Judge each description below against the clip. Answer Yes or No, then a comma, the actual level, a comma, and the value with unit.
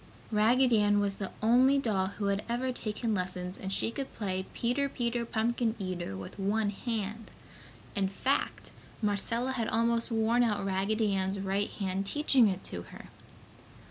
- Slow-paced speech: No, average, 160 wpm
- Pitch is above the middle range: Yes, high, 215 Hz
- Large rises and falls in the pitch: No, average, 3.3 semitones